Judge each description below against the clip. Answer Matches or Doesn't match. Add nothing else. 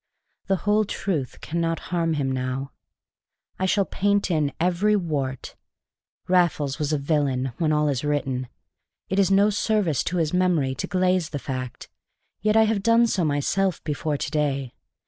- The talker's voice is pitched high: Doesn't match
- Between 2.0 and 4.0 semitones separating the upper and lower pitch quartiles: Doesn't match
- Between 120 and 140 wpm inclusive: Doesn't match